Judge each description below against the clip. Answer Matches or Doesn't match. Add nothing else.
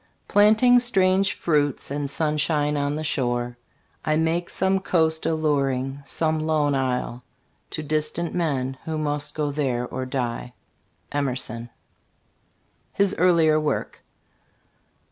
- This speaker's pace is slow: Matches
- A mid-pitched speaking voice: Matches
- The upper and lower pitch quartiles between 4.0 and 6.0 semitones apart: Doesn't match